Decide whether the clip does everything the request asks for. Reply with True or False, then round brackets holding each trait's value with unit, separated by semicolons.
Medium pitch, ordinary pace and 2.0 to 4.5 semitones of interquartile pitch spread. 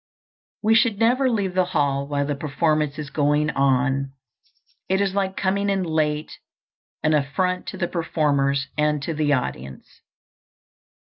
False (150 Hz; 145 wpm; 4.9 semitones)